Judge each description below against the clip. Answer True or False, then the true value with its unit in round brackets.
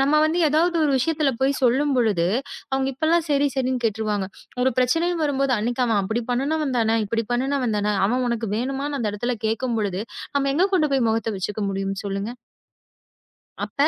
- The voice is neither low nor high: False (250 Hz)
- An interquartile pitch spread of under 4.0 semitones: False (4.3 semitones)